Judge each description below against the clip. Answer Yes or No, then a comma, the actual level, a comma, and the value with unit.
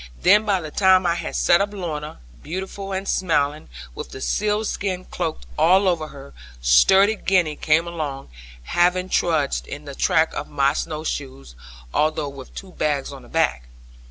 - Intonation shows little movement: No, average, 4.6 semitones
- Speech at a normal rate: Yes, average, 170 wpm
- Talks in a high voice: No, medium, 165 Hz